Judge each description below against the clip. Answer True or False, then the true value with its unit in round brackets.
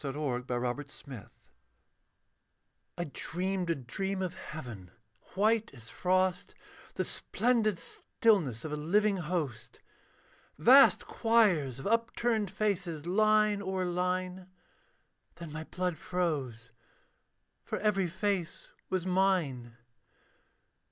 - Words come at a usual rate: False (105 wpm)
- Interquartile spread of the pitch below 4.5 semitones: False (5.2 semitones)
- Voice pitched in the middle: True (180 Hz)